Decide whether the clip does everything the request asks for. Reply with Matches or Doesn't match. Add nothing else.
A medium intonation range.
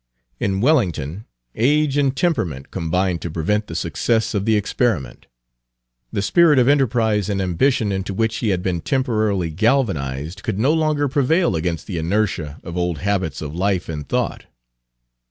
Doesn't match